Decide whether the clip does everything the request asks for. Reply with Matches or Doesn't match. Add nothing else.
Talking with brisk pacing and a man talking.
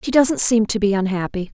Doesn't match